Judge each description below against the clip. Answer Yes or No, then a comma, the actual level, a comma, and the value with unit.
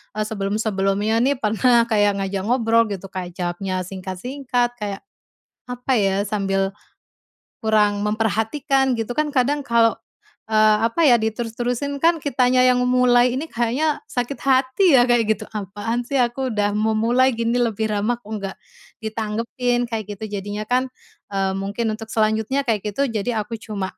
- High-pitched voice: Yes, high, 225 Hz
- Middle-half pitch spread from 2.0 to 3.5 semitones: Yes, average, 3.2 semitones